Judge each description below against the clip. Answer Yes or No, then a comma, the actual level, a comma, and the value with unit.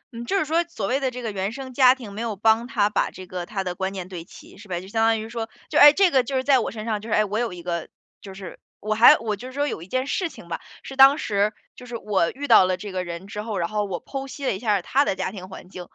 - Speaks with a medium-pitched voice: No, high, 215 Hz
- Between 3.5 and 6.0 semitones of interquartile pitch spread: Yes, average, 5.2 semitones